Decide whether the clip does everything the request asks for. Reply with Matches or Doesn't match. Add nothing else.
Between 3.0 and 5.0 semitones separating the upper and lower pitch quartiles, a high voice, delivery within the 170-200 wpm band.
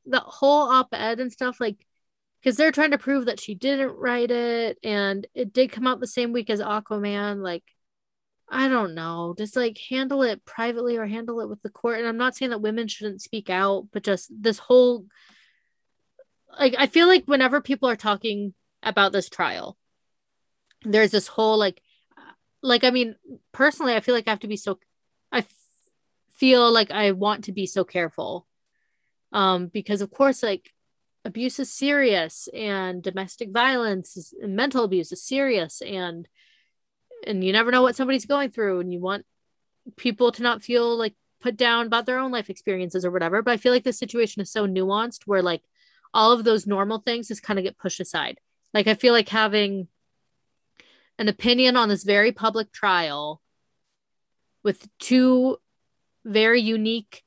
Matches